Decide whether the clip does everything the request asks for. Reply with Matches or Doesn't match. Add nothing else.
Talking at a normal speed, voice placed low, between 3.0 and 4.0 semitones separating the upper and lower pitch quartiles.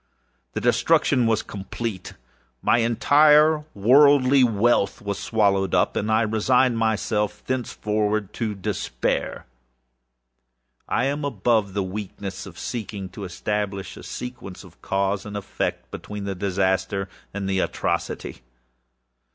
Doesn't match